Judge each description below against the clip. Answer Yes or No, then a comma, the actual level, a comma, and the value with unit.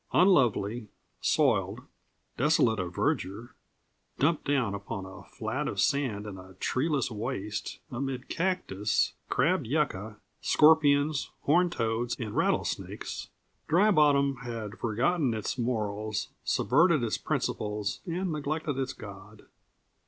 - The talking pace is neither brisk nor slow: No, slow, 115 wpm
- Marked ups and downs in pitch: Yes, wide, 6.0 semitones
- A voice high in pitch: No, low, 125 Hz